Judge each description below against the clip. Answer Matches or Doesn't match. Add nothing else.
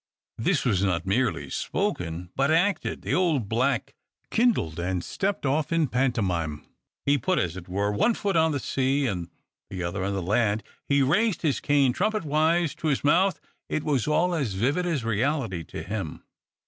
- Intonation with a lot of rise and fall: Matches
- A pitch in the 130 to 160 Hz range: Matches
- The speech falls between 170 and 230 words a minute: Matches